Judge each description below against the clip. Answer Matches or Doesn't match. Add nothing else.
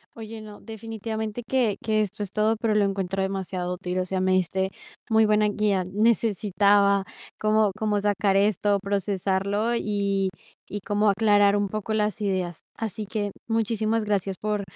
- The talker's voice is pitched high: Matches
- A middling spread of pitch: Doesn't match